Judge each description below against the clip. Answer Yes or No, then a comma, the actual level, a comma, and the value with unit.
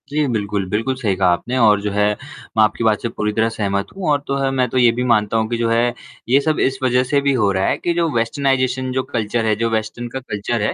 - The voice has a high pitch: No, low, 115 Hz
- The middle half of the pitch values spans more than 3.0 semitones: Yes, average, 3.6 semitones